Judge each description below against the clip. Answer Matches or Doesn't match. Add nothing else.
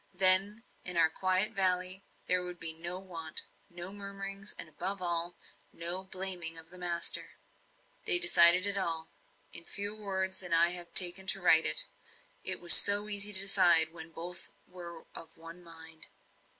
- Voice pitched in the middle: Matches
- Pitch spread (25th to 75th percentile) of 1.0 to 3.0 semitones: Matches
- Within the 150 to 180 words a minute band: Matches